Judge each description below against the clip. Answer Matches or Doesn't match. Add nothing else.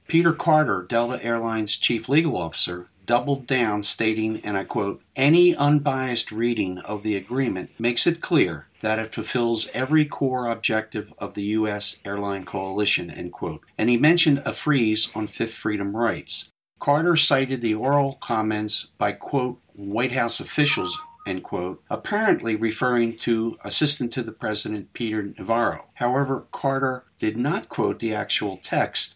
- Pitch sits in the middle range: Doesn't match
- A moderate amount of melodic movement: Matches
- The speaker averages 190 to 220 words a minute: Doesn't match